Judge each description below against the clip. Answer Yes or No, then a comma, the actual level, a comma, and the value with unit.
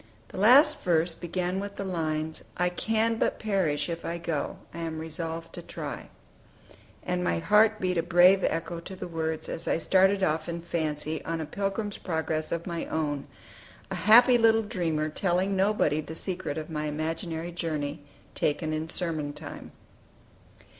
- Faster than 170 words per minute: No, average, 165 wpm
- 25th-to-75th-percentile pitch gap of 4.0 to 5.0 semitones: No, average, 3.3 semitones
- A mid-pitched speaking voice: Yes, medium, 170 Hz